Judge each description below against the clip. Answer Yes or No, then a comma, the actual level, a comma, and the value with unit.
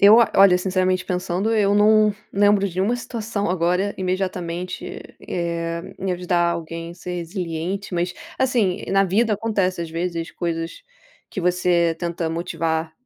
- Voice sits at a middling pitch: Yes, medium, 180 Hz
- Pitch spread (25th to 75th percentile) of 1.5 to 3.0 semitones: Yes, average, 2.7 semitones